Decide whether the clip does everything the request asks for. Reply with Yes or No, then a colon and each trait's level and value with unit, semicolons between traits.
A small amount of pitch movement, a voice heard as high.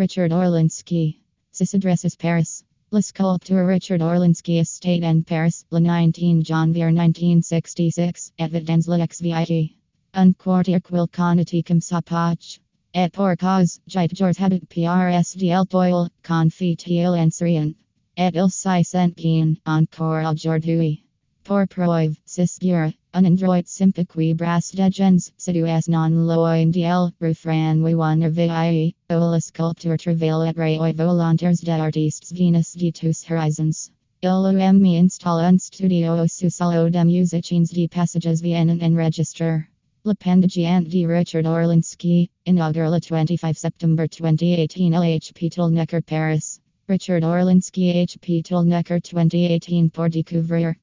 No: narrow, 1.6 semitones; medium, 170 Hz